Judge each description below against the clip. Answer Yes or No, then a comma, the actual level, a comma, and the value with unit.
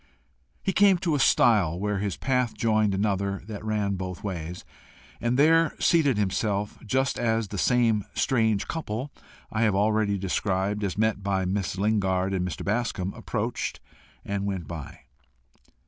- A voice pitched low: Yes, low, 105 Hz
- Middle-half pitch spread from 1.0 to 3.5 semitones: Yes, average, 3.0 semitones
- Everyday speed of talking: Yes, average, 150 wpm